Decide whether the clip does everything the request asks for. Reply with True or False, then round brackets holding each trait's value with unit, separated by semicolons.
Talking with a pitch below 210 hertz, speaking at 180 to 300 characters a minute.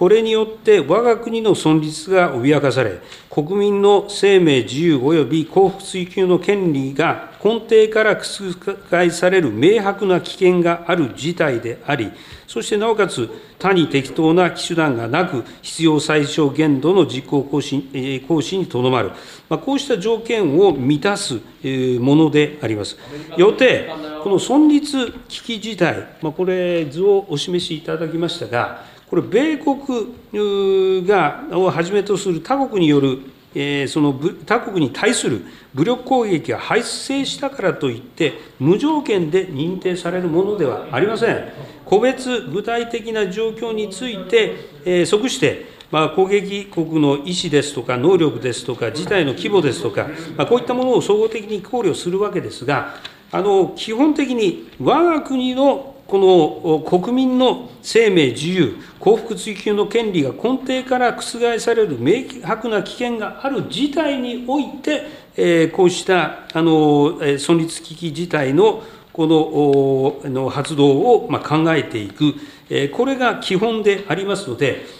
True (185 Hz; 275 characters per minute)